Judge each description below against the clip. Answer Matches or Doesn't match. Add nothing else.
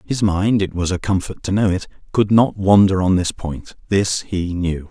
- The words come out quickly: Doesn't match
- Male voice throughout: Matches